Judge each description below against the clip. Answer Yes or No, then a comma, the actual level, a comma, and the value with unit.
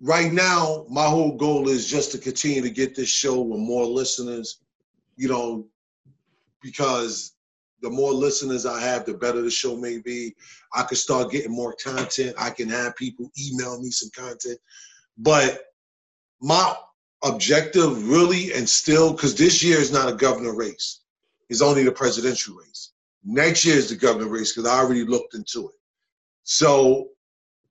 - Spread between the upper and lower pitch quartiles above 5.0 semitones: No, average, 3.7 semitones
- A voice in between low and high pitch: No, low, 130 Hz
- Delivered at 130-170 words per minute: Yes, average, 165 wpm